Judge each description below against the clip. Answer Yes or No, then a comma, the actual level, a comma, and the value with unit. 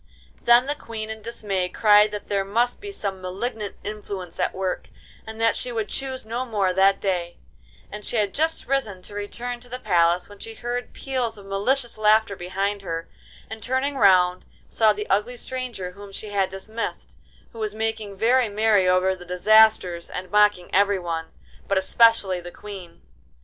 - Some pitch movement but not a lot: Yes, average, 3.3 semitones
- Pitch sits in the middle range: No, high, 210 Hz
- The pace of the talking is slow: No, average, 175 wpm